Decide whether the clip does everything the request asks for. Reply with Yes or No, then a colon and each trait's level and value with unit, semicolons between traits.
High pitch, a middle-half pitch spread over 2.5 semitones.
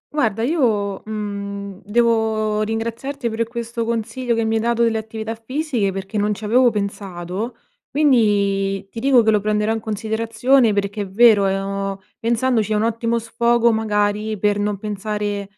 No: high, 220 Hz; narrow, 2.2 semitones